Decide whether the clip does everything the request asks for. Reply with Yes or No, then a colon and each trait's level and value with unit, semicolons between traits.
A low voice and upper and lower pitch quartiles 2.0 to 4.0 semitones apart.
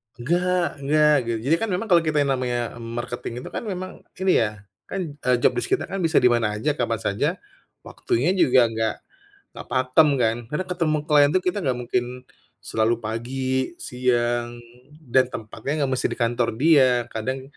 No: low, 130 Hz; average, 4.6 semitones